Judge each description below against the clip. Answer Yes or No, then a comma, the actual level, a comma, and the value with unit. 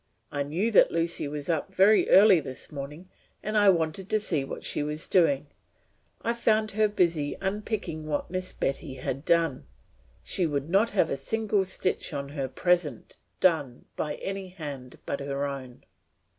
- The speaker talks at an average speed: Yes, average, 170 wpm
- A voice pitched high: No, medium, 165 Hz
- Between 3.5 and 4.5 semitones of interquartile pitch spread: No, wide, 5.4 semitones